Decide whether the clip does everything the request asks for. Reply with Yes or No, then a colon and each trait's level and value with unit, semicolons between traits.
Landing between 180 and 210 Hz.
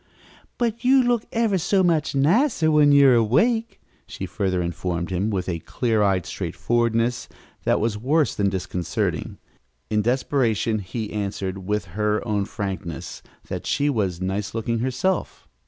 No: low, 115 Hz